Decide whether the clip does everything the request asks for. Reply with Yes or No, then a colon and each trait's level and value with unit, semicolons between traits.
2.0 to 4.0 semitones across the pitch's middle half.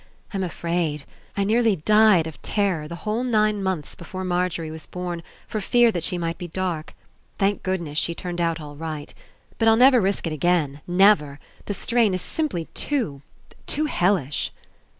No: average, 4.4 semitones